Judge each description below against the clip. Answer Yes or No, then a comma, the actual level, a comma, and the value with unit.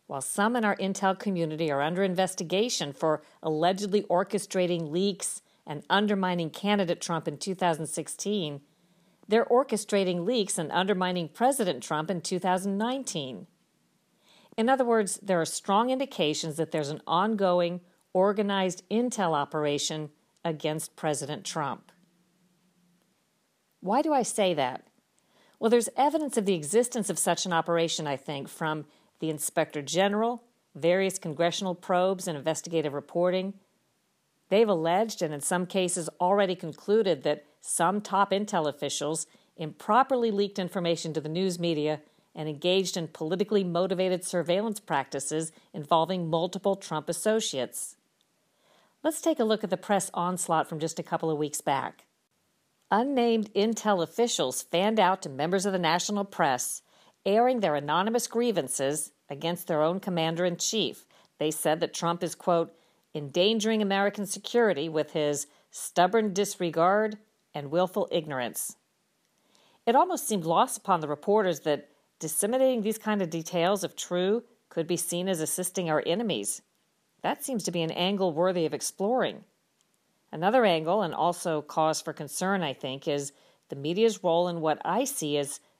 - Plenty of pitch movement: No, average, 4.2 semitones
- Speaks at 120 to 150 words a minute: Yes, average, 145 wpm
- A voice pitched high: No, medium, 180 Hz